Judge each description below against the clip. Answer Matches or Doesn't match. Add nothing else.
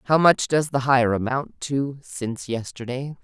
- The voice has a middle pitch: Doesn't match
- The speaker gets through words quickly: Doesn't match